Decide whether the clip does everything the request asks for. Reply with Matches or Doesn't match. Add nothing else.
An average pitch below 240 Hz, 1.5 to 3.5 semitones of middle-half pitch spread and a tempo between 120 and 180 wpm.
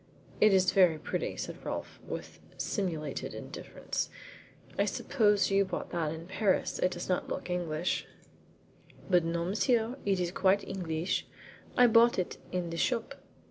Matches